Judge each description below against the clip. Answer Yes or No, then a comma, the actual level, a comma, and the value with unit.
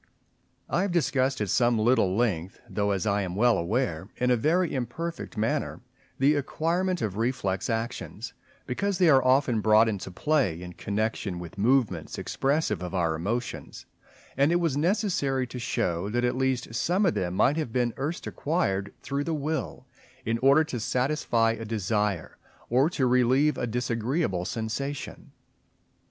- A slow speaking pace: No, average, 160 wpm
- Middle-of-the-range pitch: No, low, 120 Hz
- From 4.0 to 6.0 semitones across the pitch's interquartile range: Yes, wide, 5.5 semitones